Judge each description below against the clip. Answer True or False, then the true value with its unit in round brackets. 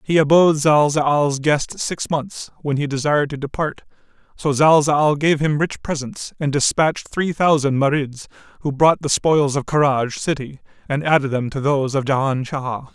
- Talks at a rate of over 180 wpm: False (170 wpm)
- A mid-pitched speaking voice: True (145 Hz)